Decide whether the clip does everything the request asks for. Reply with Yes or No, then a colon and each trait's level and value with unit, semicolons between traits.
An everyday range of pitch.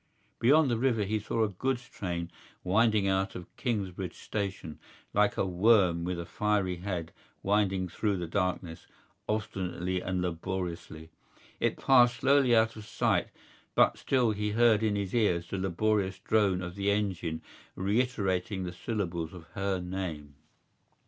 Yes: average, 3.3 semitones